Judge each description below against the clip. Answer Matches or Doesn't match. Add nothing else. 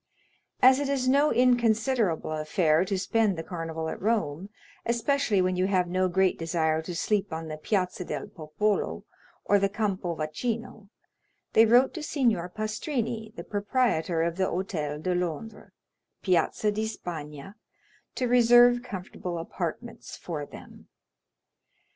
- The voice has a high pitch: Matches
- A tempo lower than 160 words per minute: Matches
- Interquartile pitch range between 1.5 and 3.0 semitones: Doesn't match